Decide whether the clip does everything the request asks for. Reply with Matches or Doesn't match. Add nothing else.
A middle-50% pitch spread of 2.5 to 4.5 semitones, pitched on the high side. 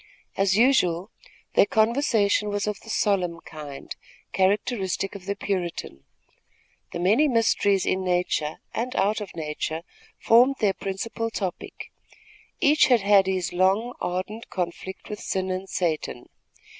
Matches